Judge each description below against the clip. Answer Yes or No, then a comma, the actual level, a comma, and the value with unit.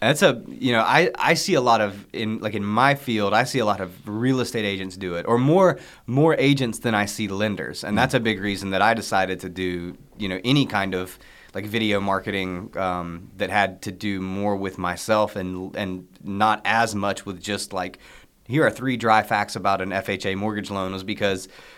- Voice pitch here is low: Yes, low, 100 Hz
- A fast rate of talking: Yes, fast, 220 wpm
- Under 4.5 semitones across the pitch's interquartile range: Yes, average, 2.7 semitones